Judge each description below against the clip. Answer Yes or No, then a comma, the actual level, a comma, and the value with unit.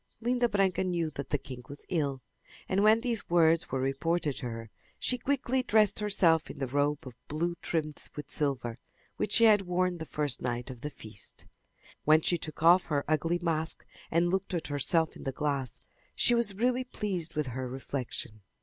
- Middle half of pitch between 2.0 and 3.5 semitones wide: No, wide, 5.6 semitones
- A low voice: No, medium, 160 Hz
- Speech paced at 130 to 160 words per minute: No, average, 190 wpm